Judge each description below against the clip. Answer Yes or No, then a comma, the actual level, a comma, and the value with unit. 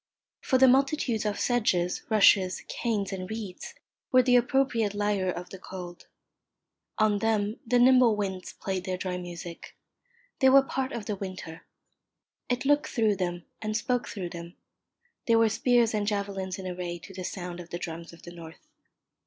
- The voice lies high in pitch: Yes, high, 205 Hz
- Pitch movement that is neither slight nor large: Yes, average, 4.5 semitones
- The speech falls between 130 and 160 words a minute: No, average, 170 wpm